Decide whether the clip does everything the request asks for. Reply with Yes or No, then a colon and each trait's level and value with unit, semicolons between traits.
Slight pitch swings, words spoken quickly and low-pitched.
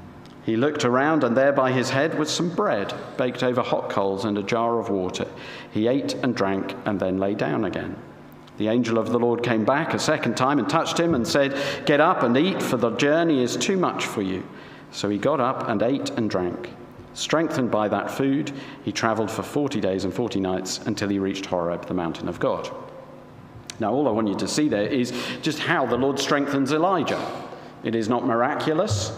No: wide, 5.4 semitones; fast, 210 wpm; low, 120 Hz